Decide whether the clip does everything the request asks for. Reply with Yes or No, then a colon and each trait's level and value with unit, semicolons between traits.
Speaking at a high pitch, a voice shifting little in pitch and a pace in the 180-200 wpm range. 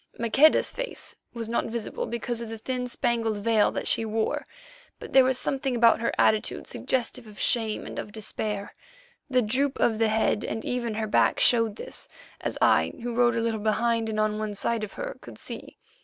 Yes: high, 230 Hz; narrow, 2.0 semitones; average, 195 wpm